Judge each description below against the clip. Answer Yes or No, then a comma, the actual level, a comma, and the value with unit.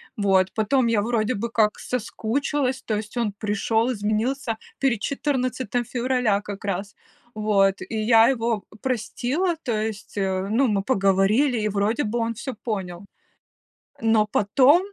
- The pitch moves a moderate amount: Yes, average, 3.4 semitones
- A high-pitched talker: Yes, high, 225 Hz